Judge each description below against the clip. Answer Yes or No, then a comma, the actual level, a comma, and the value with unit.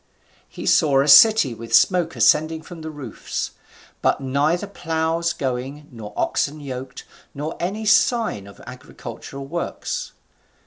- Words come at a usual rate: No, slow, 130 wpm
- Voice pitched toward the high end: No, medium, 150 Hz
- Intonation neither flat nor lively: Yes, average, 4.5 semitones